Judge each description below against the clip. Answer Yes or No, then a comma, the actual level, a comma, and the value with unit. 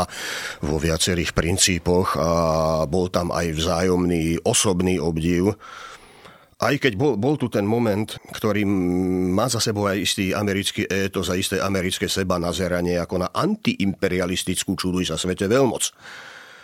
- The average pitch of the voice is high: No, very low, 95 Hz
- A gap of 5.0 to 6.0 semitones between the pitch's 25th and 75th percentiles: No, narrow, 2.5 semitones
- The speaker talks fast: No, average, 135 wpm